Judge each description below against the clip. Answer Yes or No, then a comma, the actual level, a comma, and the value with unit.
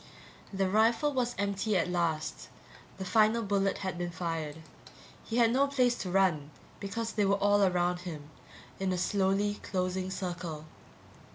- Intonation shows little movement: No, average, 3.1 semitones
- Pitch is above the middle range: Yes, high, 195 Hz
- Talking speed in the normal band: Yes, average, 155 wpm